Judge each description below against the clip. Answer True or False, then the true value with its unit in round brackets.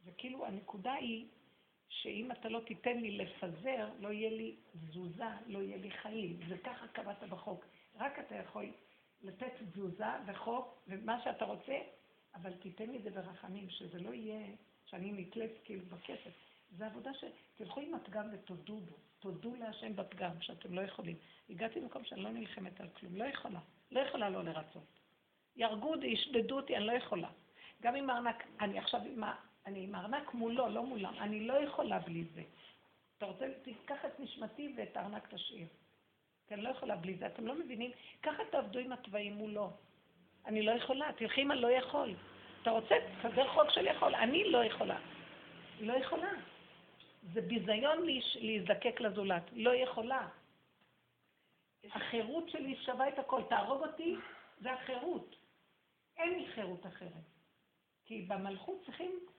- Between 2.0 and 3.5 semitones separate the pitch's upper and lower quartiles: False (4.7 semitones)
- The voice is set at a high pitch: True (225 Hz)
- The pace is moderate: False (160 wpm)